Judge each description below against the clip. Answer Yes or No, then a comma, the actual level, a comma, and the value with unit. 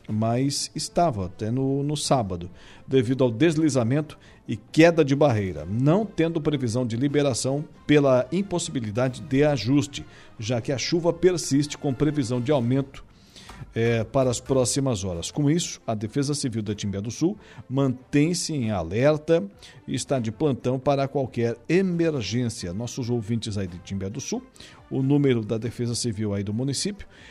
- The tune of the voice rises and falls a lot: No, average, 4.3 semitones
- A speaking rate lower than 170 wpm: Yes, average, 155 wpm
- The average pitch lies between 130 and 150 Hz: Yes, low, 135 Hz